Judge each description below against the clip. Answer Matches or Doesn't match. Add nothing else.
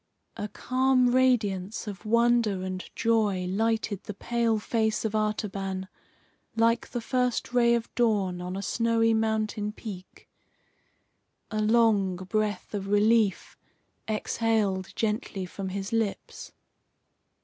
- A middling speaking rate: Doesn't match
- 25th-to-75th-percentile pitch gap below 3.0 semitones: Matches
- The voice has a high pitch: Matches